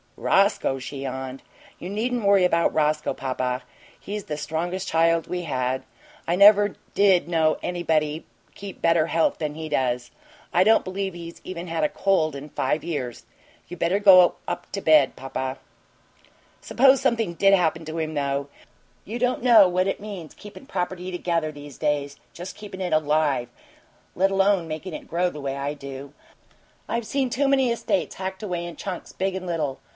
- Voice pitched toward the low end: No, medium, 170 Hz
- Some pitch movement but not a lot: Yes, average, 4.5 semitones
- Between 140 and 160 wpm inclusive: No, average, 175 wpm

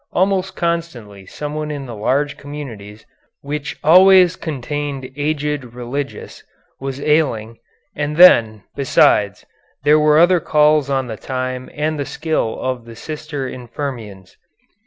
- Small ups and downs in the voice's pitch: No, average, 3.8 semitones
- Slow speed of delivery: Yes, slow, 125 wpm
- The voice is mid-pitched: Yes, medium, 145 Hz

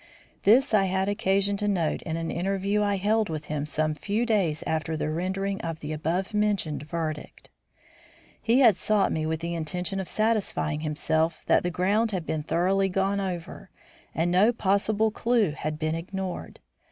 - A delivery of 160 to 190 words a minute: Yes, average, 170 wpm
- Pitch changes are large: No, average, 4.1 semitones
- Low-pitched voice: No, medium, 185 Hz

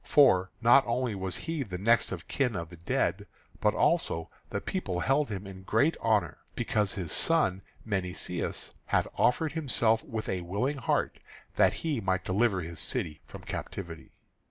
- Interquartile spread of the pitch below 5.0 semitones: No, wide, 5.4 semitones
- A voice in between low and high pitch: No, low, 100 Hz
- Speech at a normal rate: Yes, average, 165 wpm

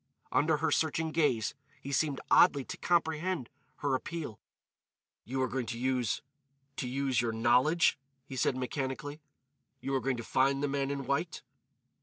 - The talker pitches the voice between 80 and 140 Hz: Yes, low, 135 Hz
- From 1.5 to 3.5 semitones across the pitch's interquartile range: Yes, narrow, 2.6 semitones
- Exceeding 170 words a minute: No, average, 155 wpm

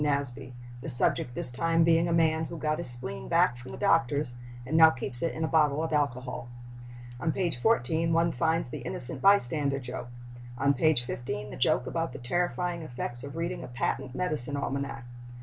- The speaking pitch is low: No, medium, 145 Hz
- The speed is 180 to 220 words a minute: Yes, average, 190 wpm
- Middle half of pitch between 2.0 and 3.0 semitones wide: No, average, 4.8 semitones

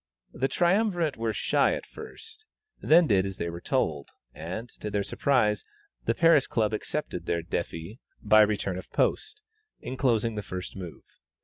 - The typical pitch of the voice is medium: No, low, 110 Hz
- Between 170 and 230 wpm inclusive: No, average, 155 wpm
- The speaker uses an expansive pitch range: Yes, wide, 7.1 semitones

